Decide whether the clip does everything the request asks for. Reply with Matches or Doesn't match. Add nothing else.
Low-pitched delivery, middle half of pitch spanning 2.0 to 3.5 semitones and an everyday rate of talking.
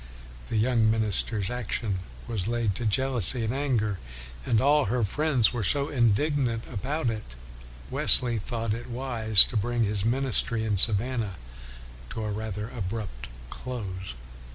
Matches